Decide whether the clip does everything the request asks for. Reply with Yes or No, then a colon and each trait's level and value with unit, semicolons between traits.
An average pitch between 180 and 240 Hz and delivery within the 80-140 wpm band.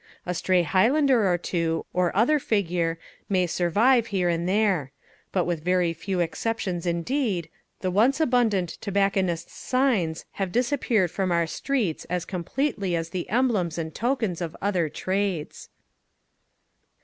Yes: medium, 185 Hz; slow, 135 wpm